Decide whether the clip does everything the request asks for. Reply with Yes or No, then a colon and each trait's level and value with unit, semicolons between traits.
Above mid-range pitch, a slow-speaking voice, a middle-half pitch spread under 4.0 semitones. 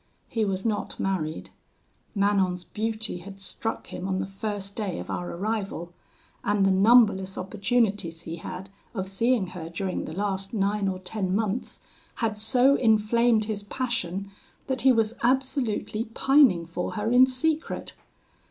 No: high, 205 Hz; average, 150 wpm; average, 3.1 semitones